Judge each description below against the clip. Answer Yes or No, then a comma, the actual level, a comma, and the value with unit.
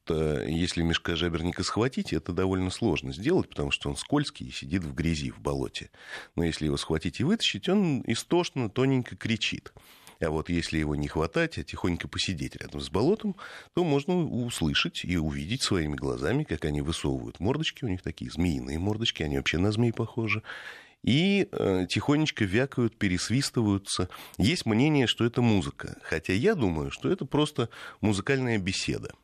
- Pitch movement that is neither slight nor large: No, wide, 7.6 semitones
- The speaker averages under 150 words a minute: No, fast, 160 wpm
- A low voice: Yes, very low, 95 Hz